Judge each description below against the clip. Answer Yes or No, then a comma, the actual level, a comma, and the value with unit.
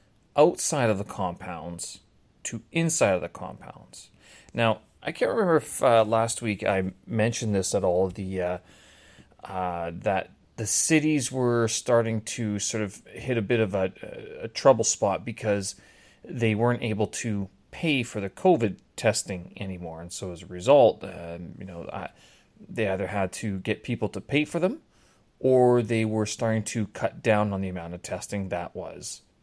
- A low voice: Yes, low, 105 Hz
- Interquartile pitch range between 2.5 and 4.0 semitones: Yes, average, 3.6 semitones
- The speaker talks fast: No, average, 175 wpm